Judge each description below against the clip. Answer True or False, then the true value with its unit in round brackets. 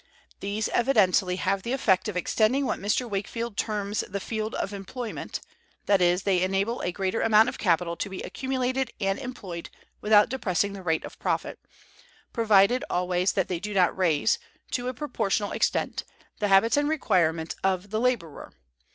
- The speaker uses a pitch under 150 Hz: False (200 Hz)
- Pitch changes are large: False (3.8 semitones)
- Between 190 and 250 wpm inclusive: False (170 wpm)